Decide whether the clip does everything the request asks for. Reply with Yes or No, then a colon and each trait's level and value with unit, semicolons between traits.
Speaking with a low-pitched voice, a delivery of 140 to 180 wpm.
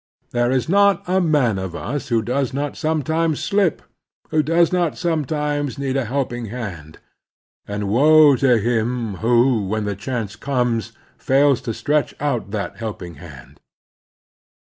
Yes: low, 130 Hz; average, 145 wpm